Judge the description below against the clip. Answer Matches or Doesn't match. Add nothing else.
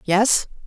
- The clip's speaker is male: Doesn't match